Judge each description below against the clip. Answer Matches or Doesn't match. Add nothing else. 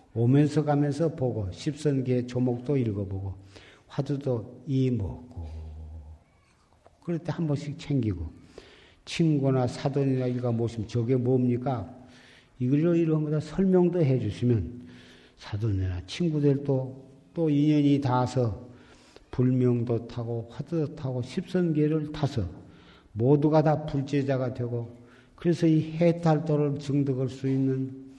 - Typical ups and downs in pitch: Matches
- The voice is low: Matches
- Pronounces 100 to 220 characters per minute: Doesn't match